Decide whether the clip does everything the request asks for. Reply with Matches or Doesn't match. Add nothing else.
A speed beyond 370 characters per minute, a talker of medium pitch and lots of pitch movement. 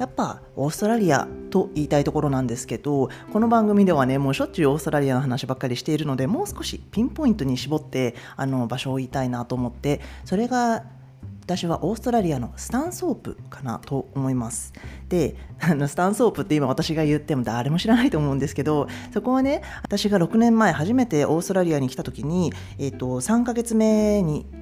Matches